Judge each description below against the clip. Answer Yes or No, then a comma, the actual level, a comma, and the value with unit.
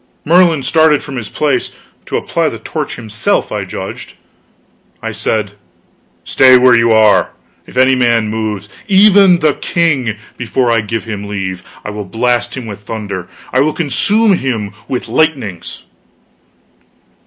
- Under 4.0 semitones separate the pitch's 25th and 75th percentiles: No, wide, 5.5 semitones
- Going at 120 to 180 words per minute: Yes, average, 145 wpm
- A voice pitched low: Yes, low, 120 Hz